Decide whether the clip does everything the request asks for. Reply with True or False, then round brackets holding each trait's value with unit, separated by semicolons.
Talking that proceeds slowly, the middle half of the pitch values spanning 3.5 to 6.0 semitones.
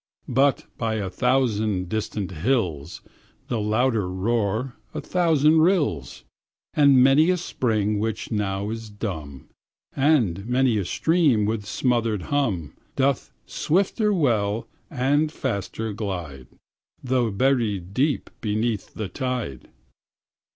True (115 wpm; 5.1 semitones)